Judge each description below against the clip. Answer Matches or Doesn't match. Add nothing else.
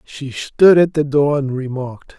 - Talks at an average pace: Matches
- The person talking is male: Matches